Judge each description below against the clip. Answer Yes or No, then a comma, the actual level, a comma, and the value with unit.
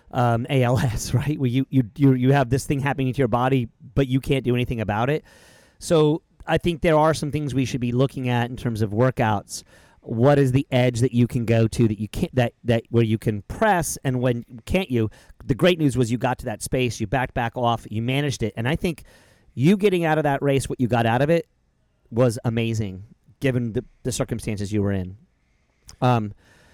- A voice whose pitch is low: Yes, low, 125 Hz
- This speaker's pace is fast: Yes, fast, 225 wpm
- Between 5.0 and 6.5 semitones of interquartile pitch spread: No, average, 3.2 semitones